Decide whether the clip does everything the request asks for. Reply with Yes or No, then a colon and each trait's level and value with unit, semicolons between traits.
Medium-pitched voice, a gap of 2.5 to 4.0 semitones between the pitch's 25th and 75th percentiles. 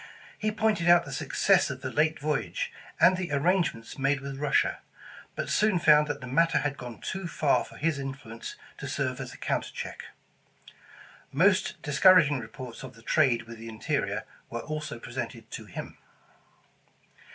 No: medium, 145 Hz; average, 4.8 semitones